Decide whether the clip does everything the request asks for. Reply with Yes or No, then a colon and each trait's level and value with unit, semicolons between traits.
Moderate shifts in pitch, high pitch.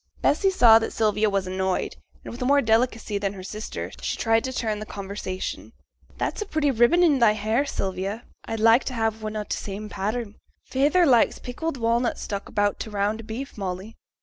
Yes: average, 3.3 semitones; high, 220 Hz